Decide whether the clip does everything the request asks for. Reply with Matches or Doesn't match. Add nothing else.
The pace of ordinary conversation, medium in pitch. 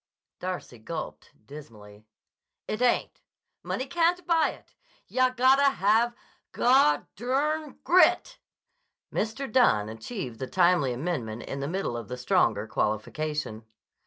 Doesn't match